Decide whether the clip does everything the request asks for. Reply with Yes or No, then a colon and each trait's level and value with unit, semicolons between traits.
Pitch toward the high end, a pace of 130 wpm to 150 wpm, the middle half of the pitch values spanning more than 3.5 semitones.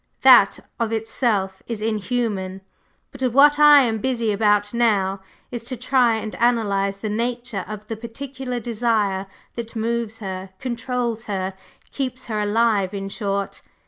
No: high, 225 Hz; average, 145 wpm; average, 3.0 semitones